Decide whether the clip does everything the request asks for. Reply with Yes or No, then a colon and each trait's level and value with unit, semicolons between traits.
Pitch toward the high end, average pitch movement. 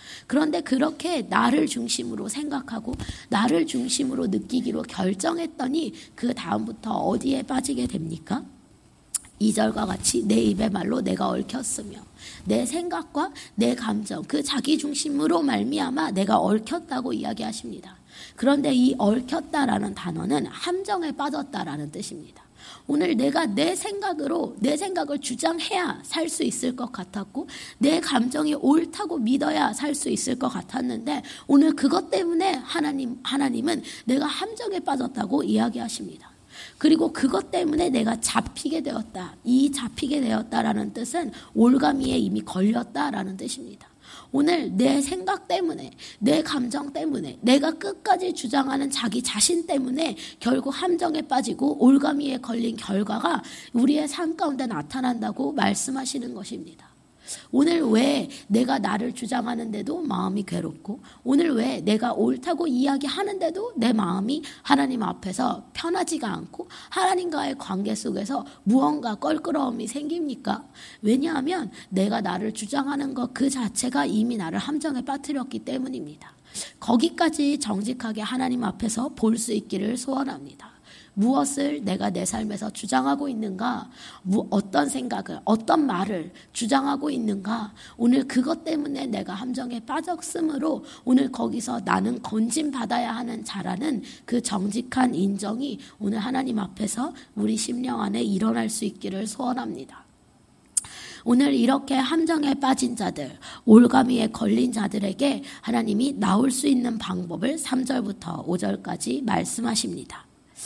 Yes: very high, 260 Hz; average, 4.5 semitones